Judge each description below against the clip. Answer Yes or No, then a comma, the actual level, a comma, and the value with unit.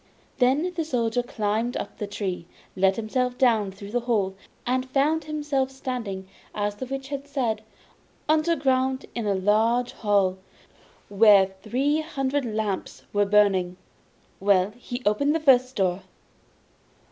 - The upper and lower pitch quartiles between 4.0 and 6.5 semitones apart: Yes, average, 4.6 semitones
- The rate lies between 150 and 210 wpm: No, average, 140 wpm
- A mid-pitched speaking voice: No, high, 235 Hz